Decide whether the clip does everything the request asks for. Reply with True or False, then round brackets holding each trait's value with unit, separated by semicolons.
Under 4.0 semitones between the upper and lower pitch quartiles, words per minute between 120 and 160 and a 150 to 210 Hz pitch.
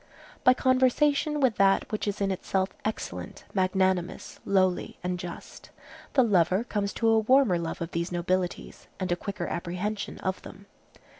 True (3.5 semitones; 155 wpm; 190 Hz)